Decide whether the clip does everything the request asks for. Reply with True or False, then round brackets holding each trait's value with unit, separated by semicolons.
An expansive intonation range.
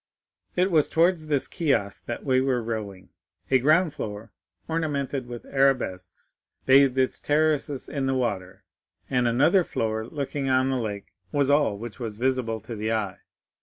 False (4.4 semitones)